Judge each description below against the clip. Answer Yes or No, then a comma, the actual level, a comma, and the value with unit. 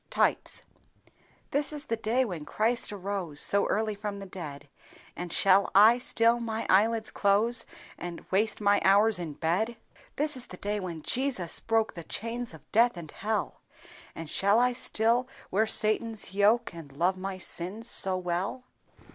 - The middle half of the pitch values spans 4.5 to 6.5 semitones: No, average, 3.8 semitones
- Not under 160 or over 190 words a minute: Yes, average, 165 wpm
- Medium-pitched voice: No, high, 205 Hz